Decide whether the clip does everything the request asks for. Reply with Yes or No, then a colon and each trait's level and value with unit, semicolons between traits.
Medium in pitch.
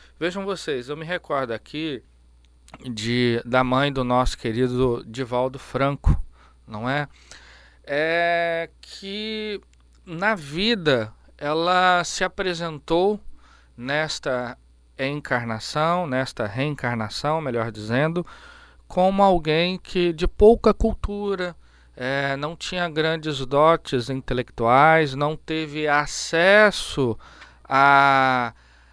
Yes: medium, 145 Hz